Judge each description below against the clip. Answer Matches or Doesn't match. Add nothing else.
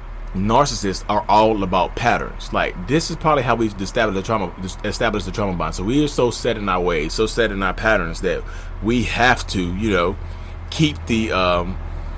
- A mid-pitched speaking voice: Doesn't match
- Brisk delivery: Doesn't match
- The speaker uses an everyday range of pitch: Matches